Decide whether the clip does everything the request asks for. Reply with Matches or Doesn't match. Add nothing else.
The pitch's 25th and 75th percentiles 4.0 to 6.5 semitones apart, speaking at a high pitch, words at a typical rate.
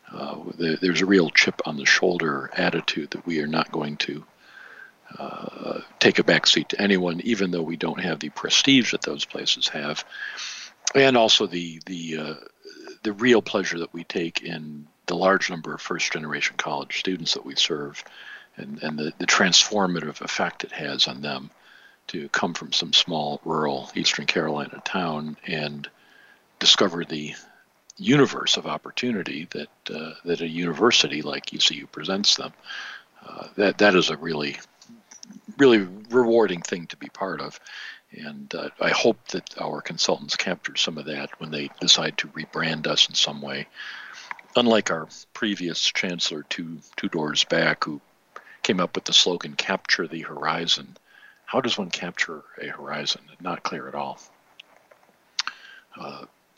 Doesn't match